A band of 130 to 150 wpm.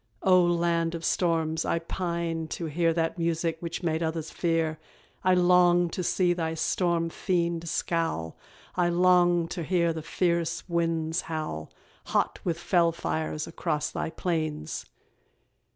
Yes: average, 140 wpm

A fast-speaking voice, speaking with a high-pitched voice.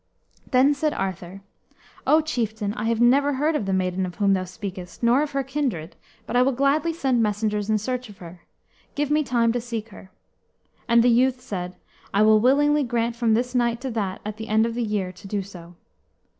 Yes: fast, 210 wpm; high, 230 Hz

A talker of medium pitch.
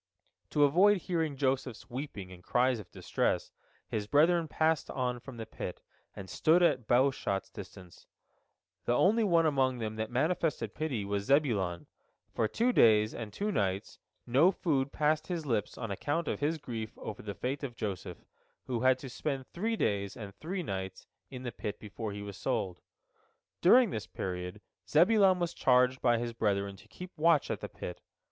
No: low, 125 Hz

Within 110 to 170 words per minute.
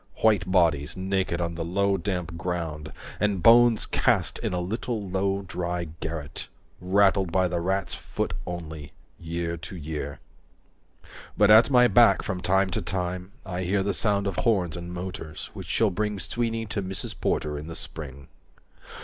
Yes: average, 165 wpm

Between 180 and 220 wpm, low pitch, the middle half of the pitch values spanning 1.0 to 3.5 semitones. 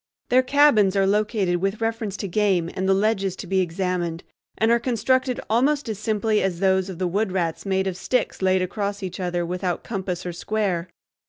No: average, 195 wpm; high, 195 Hz; average, 3.1 semitones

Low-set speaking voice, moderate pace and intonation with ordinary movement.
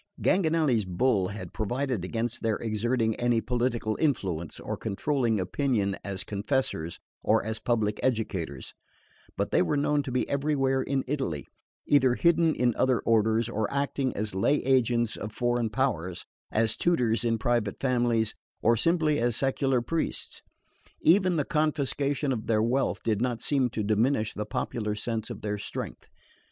Yes: low, 120 Hz; average, 155 wpm; average, 4.0 semitones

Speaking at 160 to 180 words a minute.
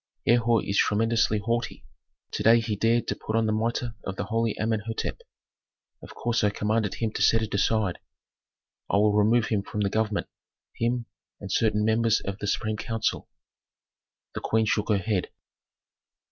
Yes: average, 170 wpm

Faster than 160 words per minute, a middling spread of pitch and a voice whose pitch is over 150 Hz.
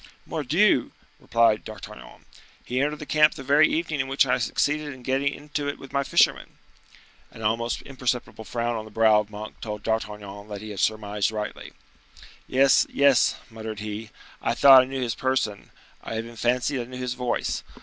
No: average, 180 wpm; average, 3.9 semitones; low, 120 Hz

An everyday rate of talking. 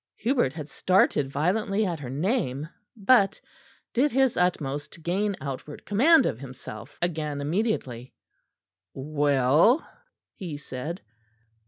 No: slow, 115 wpm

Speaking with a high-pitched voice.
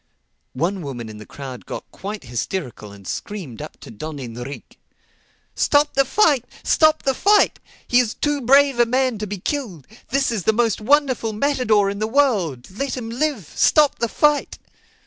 Yes: high, 220 Hz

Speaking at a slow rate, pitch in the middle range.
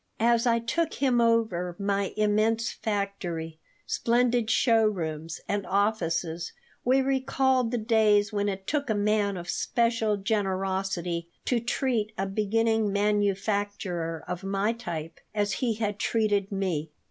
No: slow, 130 wpm; high, 205 Hz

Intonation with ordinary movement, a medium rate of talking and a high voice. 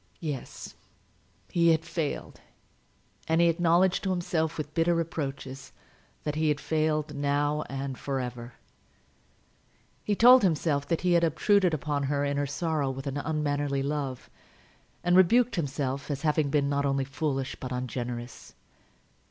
No: average, 3.2 semitones; average, 145 wpm; medium, 150 Hz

